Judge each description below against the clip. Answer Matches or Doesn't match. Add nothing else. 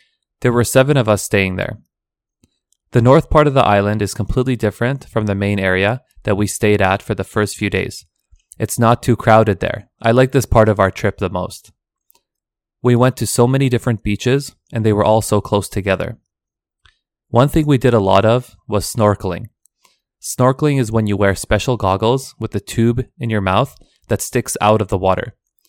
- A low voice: Matches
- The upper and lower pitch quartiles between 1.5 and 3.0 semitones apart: Doesn't match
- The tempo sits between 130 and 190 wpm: Doesn't match